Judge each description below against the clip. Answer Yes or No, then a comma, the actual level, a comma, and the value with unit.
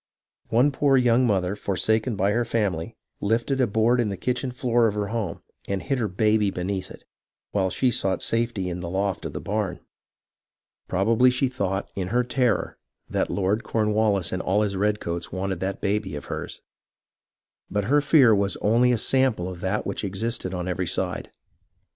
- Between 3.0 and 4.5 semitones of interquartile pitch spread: Yes, average, 3.8 semitones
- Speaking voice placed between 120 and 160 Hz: No, low, 105 Hz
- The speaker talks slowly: No, average, 180 wpm